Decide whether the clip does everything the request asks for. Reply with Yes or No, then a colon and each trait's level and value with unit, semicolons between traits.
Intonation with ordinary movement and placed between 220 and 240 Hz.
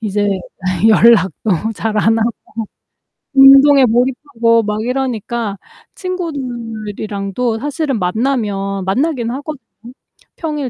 Yes: average, 4.3 semitones; high, 230 Hz